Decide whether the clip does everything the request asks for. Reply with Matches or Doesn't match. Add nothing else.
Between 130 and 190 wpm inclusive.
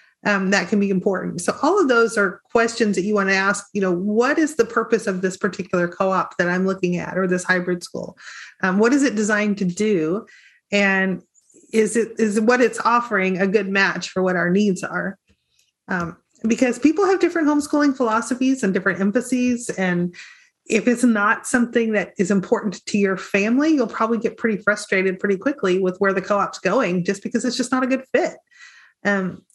Doesn't match